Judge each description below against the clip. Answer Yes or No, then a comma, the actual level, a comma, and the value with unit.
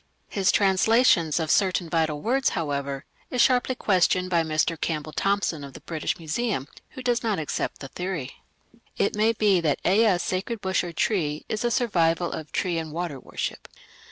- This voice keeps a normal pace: Yes, average, 180 wpm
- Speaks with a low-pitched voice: No, medium, 180 Hz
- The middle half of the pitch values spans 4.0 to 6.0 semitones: Yes, average, 5.0 semitones